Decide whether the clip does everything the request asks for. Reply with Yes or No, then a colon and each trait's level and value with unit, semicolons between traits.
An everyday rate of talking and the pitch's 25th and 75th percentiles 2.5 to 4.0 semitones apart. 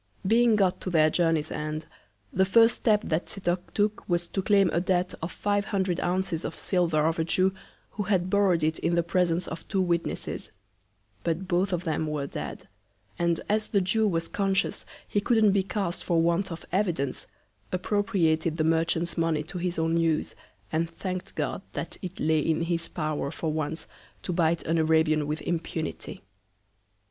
Yes: average, 180 wpm; average, 2.9 semitones